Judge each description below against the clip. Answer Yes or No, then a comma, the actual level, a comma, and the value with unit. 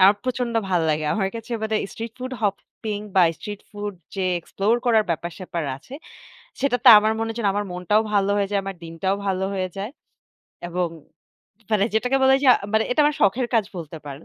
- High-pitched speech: Yes, high, 205 Hz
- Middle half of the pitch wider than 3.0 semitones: Yes, average, 3.4 semitones